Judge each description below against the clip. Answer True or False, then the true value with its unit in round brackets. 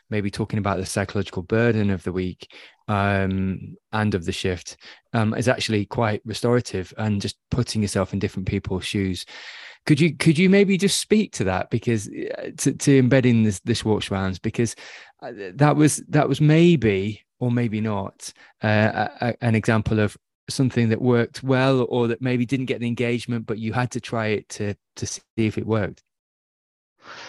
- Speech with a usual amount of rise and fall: True (3.5 semitones)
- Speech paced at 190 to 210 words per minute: False (180 wpm)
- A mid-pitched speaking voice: False (110 Hz)